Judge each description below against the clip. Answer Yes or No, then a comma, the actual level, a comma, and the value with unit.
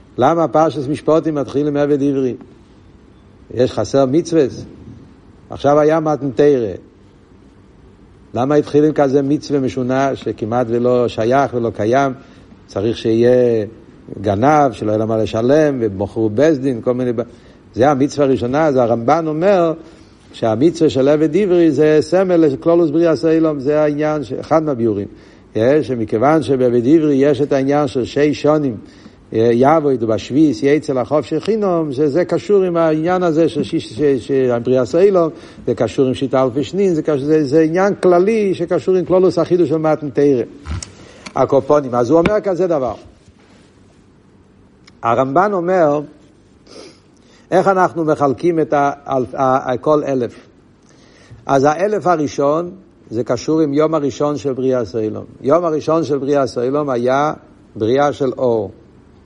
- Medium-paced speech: Yes, average, 130 wpm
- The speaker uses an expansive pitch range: No, average, 4.2 semitones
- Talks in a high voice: No, medium, 145 Hz